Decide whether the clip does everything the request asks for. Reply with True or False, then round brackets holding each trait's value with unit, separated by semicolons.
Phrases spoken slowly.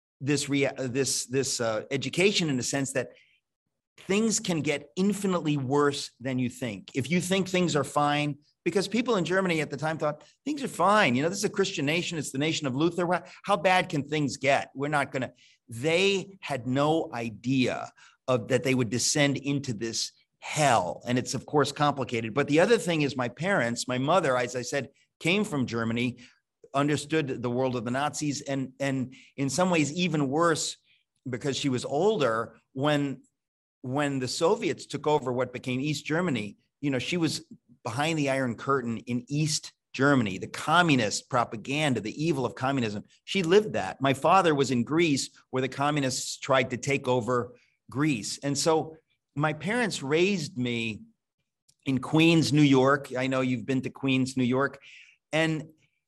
False (180 wpm)